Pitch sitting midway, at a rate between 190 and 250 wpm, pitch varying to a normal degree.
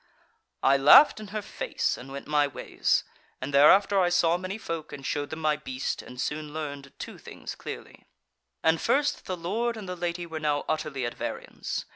Yes: medium, 155 Hz; average, 195 wpm; average, 4.2 semitones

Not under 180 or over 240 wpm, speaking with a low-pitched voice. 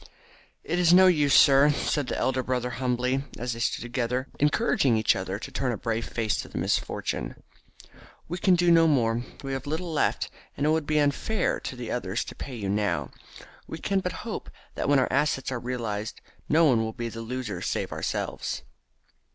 Yes: average, 195 wpm; low, 130 Hz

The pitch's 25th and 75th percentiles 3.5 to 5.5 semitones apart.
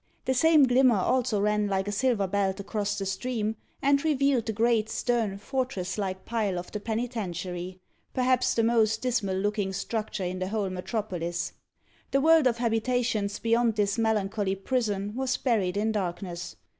Yes: average, 3.8 semitones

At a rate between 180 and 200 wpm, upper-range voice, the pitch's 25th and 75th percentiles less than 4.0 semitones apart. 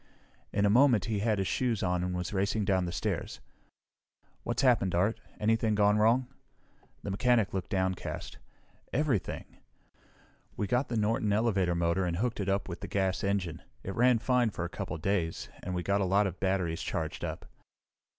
No: average, 185 wpm; low, 100 Hz; average, 3.4 semitones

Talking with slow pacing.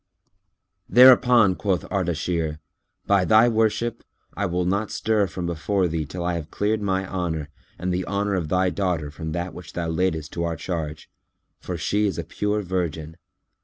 No: average, 170 wpm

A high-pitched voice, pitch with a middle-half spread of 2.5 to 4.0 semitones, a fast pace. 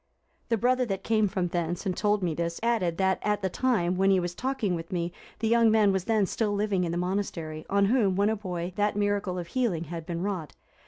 Yes: high, 195 Hz; average, 3.3 semitones; fast, 235 wpm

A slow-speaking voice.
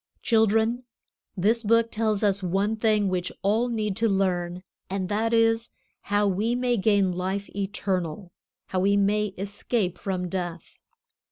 No: average, 145 wpm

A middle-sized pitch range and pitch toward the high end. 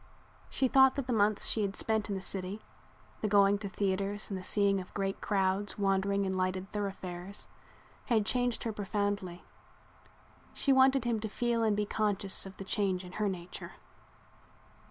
No: narrow, 2.1 semitones; high, 200 Hz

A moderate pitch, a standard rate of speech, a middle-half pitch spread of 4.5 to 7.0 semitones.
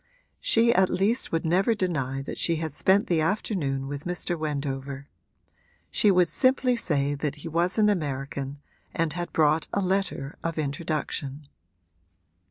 Yes: medium, 160 Hz; average, 150 wpm; average, 4.8 semitones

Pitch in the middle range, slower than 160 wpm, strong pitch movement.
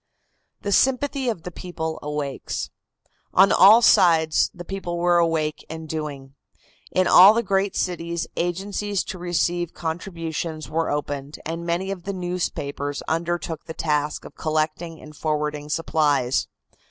No: medium, 165 Hz; average, 140 wpm; average, 2.9 semitones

